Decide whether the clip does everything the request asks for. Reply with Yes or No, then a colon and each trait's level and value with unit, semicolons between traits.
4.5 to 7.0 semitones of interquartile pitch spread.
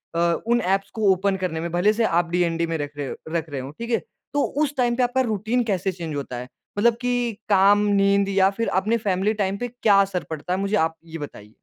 Yes: average, 4.8 semitones